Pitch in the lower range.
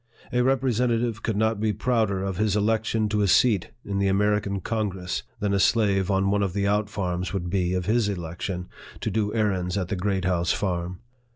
Yes: low, 100 Hz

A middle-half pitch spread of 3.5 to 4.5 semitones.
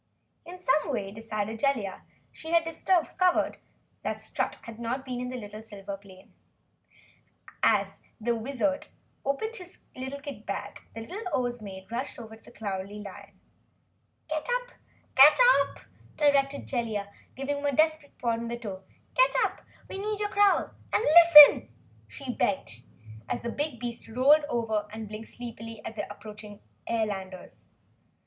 No: wide, 5.4 semitones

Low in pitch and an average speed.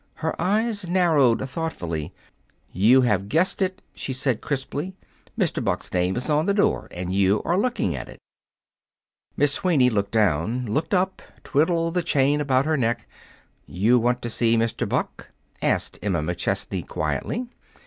Yes: low, 130 Hz; average, 155 wpm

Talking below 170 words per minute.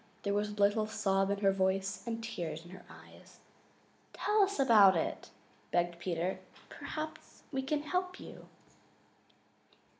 Yes: average, 150 wpm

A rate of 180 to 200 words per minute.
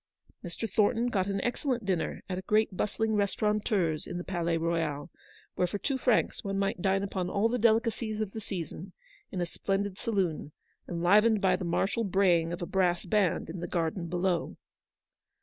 Yes: average, 185 wpm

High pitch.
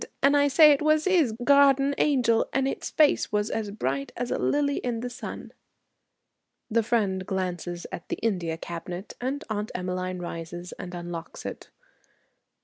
Yes: high, 220 Hz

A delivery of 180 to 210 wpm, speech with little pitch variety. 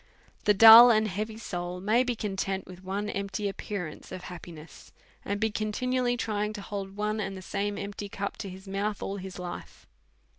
Yes: average, 185 wpm; narrow, 2.0 semitones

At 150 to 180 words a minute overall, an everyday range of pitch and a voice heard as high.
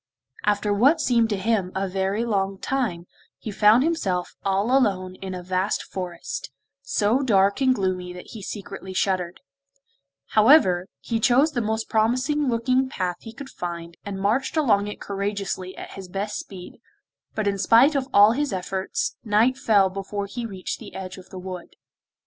Yes: average, 170 wpm; average, 4.0 semitones; high, 205 Hz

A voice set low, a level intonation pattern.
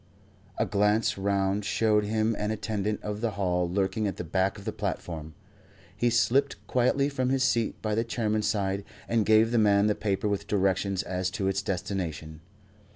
Yes: low, 105 Hz; narrow, 2.3 semitones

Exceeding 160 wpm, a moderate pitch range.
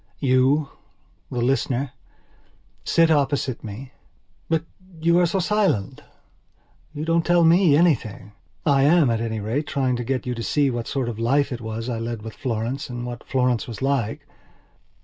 Yes: average, 170 wpm; average, 4.4 semitones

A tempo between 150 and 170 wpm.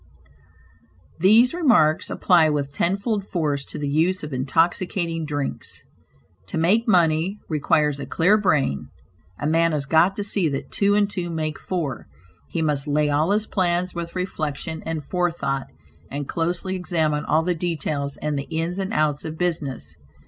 Yes: average, 160 wpm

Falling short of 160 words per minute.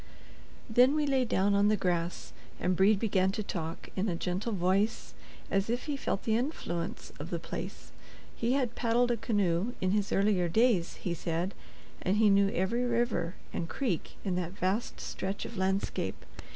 No: average, 180 wpm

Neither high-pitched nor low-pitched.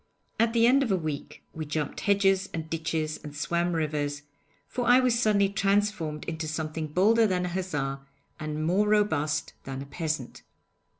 Yes: medium, 165 Hz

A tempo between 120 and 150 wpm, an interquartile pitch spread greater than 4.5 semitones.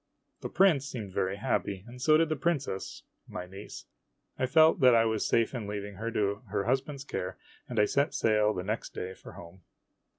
No: average, 200 wpm; average, 5.2 semitones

